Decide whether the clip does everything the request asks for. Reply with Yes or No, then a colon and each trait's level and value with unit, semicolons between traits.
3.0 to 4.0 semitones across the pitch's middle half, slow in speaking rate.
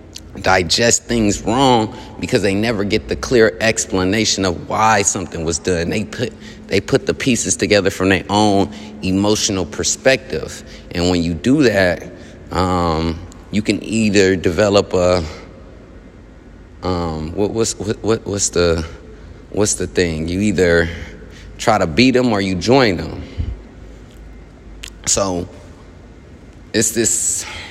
Yes: average, 3.7 semitones; slow, 130 wpm